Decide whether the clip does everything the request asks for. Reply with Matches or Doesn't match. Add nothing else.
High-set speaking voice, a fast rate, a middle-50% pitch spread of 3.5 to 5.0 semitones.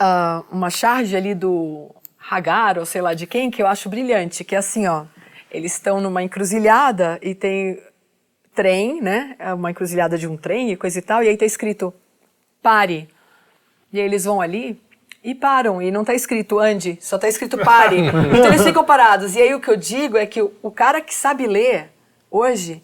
Matches